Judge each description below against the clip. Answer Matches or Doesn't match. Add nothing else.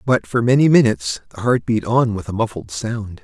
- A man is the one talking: Matches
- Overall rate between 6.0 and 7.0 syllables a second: Doesn't match